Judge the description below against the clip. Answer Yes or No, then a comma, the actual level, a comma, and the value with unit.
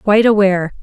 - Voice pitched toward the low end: No, high, 200 Hz